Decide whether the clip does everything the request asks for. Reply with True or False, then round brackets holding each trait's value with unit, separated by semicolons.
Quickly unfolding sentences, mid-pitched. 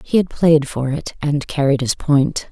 True (215 wpm; 145 Hz)